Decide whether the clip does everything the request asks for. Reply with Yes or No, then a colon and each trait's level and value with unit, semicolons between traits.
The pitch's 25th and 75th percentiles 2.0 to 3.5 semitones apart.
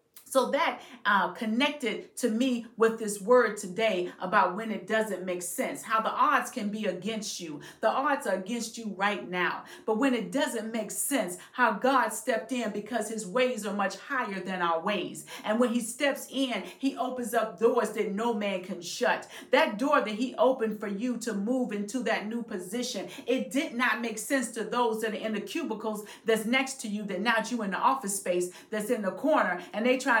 Yes: average, 3.2 semitones